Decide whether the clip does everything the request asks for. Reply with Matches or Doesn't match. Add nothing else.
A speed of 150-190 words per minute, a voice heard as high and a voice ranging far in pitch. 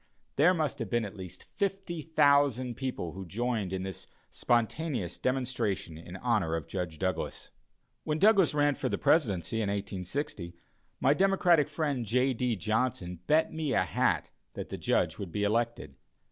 Doesn't match